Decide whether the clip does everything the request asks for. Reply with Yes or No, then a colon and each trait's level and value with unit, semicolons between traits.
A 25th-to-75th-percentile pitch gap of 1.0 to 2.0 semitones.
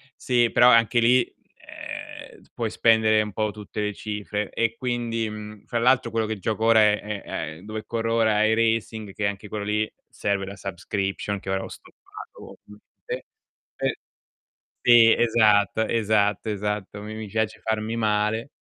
Yes: narrow, 1.7 semitones